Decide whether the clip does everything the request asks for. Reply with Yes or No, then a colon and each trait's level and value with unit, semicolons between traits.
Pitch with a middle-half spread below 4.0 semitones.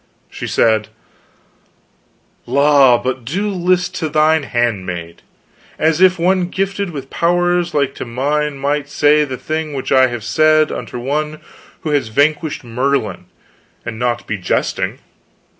No: average, 4.5 semitones